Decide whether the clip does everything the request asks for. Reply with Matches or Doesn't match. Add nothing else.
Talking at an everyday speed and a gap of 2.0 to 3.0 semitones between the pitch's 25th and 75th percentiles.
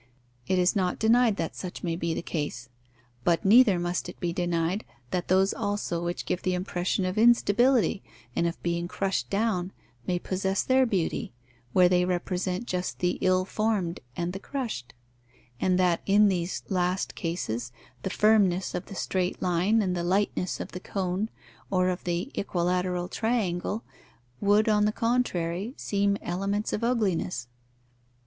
Matches